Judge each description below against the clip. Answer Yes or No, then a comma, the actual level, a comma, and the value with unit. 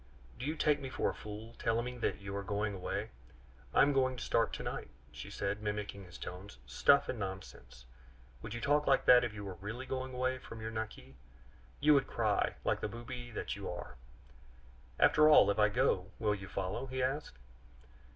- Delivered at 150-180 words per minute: No, fast, 205 wpm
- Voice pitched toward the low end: Yes, low, 110 Hz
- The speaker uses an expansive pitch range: No, average, 4.4 semitones